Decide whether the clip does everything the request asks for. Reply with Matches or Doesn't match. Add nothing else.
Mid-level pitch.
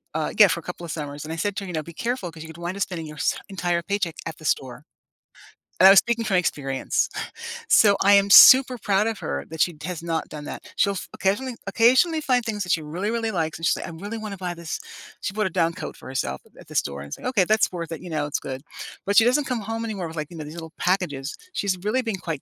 Matches